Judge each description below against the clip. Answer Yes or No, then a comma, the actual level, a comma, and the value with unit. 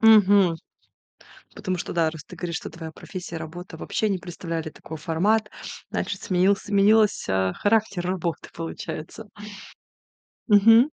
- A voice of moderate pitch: Yes, medium, 180 Hz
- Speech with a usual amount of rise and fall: Yes, average, 4.0 semitones